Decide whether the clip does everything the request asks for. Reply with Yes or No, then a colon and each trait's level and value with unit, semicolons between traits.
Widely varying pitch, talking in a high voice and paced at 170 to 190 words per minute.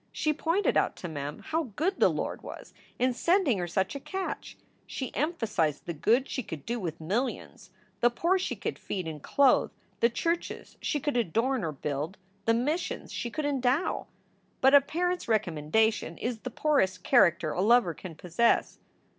Yes: wide, 8.3 semitones; high, 235 Hz; average, 180 wpm